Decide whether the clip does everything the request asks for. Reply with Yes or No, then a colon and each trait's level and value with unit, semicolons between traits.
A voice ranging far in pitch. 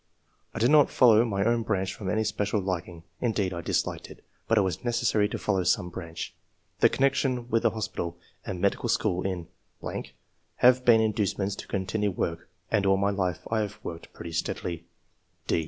No: average, 3.5 semitones